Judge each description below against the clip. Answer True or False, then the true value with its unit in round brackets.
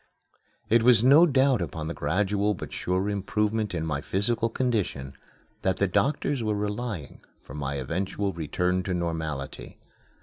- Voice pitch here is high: False (100 Hz)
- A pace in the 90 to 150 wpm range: True (145 wpm)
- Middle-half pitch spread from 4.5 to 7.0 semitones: True (5.3 semitones)